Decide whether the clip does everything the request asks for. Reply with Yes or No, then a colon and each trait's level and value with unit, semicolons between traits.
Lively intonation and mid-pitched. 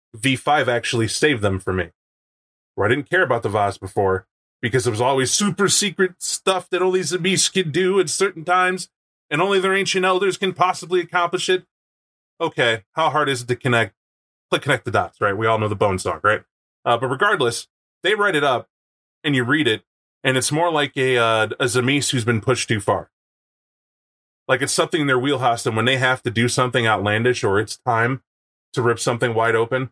No: wide, 7.7 semitones; low, 130 Hz